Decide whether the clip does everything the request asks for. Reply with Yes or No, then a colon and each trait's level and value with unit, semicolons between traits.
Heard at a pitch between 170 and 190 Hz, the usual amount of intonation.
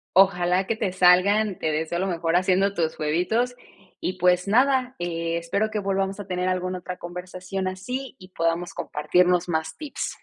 No: medium, 185 Hz; narrow, 2.2 semitones